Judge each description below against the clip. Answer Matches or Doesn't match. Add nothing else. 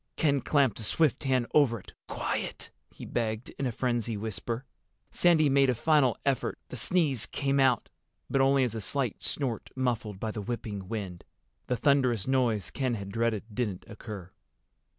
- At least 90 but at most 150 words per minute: Doesn't match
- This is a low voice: Matches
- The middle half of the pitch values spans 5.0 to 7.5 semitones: Doesn't match